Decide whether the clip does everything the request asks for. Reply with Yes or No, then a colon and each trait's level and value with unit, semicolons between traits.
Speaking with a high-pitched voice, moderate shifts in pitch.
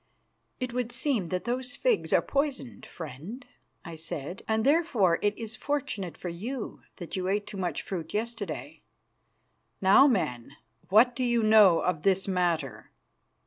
No: high, 205 Hz; wide, 5.8 semitones